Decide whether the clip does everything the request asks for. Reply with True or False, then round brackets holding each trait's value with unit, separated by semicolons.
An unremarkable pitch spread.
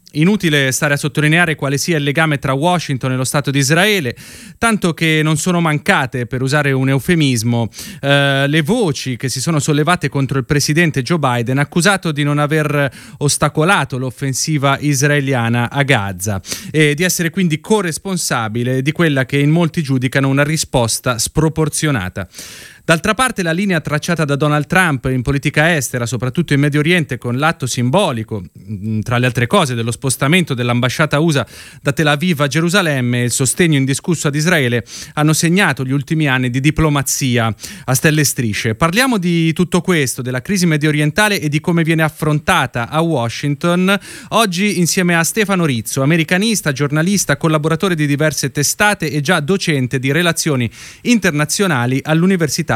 True (4.1 semitones)